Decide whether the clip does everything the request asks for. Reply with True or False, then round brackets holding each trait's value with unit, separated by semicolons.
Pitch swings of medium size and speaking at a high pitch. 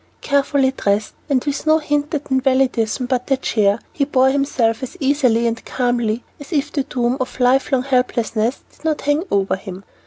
True (3.2 semitones; 260 Hz)